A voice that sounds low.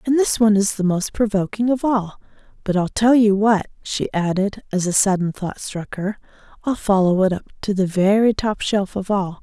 No: high, 205 Hz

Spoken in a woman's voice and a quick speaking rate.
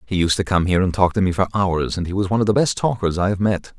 No: male; fast, 350 wpm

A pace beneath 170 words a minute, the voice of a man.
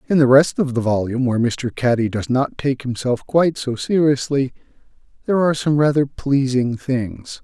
No: average, 180 wpm; male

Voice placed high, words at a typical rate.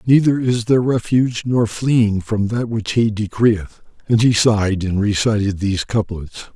No: low, 110 Hz; average, 165 wpm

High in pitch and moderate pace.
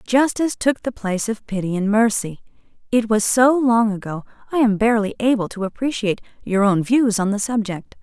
Yes: high, 220 Hz; average, 185 wpm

